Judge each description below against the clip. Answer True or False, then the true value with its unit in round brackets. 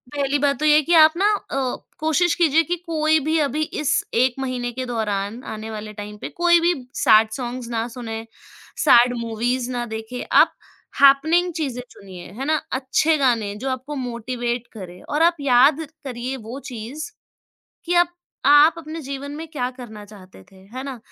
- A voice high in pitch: True (260 Hz)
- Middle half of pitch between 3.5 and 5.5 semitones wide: True (4.7 semitones)